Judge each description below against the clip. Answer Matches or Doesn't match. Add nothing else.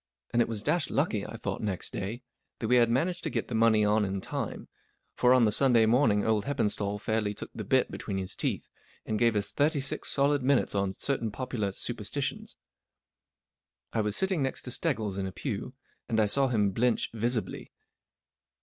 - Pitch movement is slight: Doesn't match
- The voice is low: Matches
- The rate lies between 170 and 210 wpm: Matches